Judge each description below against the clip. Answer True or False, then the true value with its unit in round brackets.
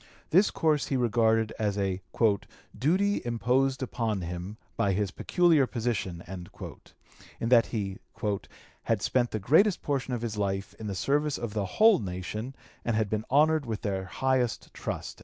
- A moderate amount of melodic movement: True (5.0 semitones)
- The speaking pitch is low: True (115 Hz)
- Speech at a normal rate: True (160 wpm)